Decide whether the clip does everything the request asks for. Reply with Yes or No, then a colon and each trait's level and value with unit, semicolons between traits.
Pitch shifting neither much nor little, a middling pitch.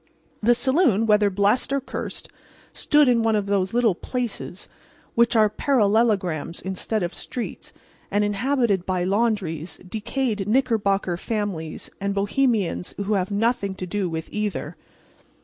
No: average, 3.5 semitones; high, 205 Hz